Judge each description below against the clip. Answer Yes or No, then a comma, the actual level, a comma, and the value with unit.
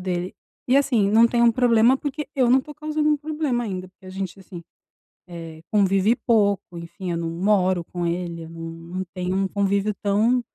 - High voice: Yes, high, 200 Hz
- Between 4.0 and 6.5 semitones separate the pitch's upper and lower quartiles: Yes, average, 5.1 semitones